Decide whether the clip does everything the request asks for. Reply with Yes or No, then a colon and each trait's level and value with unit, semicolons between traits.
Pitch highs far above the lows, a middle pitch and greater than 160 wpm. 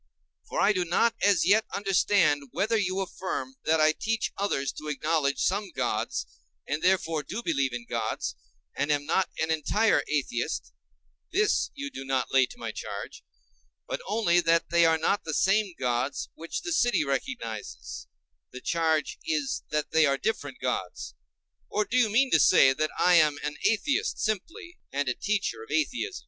Yes: wide, 6.8 semitones; medium, 165 Hz; average, 170 wpm